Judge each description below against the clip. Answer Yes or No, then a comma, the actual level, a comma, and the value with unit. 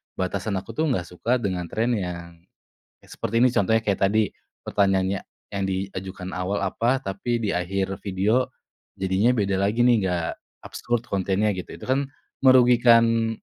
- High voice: No, low, 100 Hz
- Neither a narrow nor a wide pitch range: Yes, average, 3.7 semitones